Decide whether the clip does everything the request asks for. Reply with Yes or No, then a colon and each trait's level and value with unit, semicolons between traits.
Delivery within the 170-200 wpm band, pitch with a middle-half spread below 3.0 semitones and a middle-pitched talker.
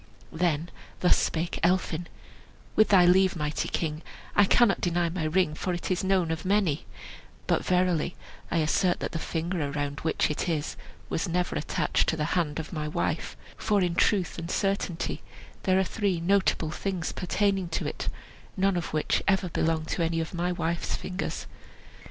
Yes: average, 175 wpm; narrow, 2.6 semitones; medium, 175 Hz